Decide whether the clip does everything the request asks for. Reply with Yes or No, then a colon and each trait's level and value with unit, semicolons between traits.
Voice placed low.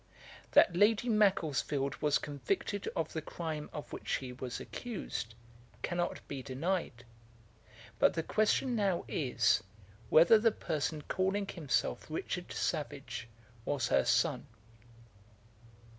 No: medium, 155 Hz